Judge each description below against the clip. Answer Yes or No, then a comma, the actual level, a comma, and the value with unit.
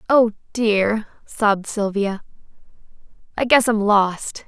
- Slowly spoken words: Yes, slow, 105 wpm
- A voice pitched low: No, high, 210 Hz